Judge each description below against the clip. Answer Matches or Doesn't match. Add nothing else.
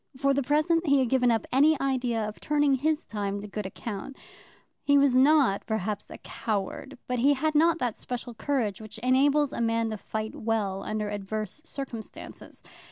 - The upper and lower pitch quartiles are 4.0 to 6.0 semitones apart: Matches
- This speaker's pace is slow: Doesn't match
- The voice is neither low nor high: Doesn't match